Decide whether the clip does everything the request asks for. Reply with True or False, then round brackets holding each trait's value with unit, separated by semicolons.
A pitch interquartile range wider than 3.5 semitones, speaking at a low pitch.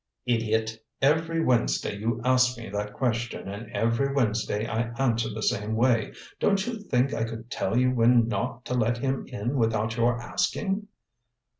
False (2.4 semitones; 115 Hz)